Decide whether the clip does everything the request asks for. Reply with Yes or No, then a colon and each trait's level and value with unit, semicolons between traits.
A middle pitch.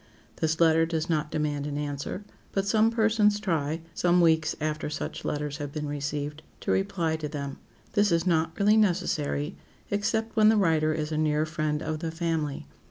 Yes: medium, 160 Hz